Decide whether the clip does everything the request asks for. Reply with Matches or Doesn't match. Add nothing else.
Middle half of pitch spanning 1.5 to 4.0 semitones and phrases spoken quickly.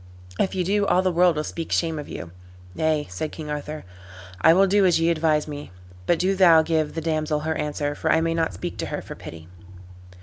Matches